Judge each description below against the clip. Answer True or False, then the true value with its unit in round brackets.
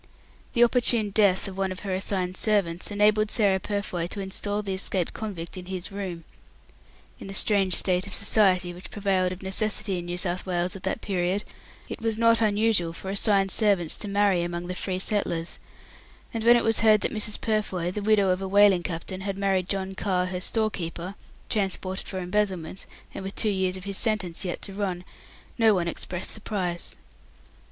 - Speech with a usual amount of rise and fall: False (2.3 semitones)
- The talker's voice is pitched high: True (195 Hz)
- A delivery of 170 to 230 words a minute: True (190 wpm)